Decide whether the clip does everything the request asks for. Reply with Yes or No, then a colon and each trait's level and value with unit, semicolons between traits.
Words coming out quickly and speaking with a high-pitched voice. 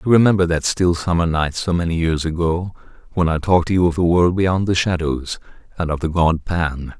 No: fast, 225 wpm; very low, 85 Hz